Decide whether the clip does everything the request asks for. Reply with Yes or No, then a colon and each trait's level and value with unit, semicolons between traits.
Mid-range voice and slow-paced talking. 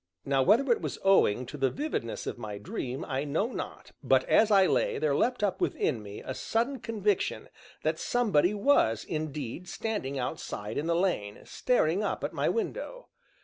No: medium, 170 Hz; average, 180 wpm